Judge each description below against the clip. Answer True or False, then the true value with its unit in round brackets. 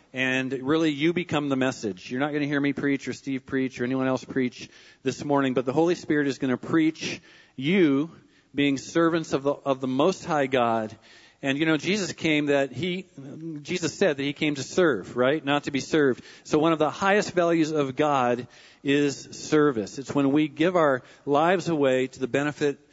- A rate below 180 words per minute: False (205 wpm)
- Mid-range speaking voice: True (145 Hz)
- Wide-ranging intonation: False (3.2 semitones)